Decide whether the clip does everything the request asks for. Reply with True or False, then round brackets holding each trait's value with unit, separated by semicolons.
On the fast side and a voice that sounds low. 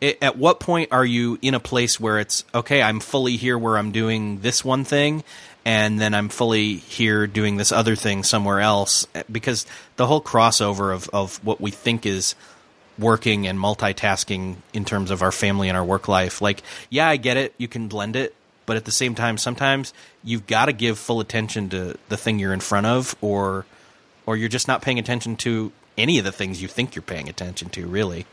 True (210 wpm; 110 Hz)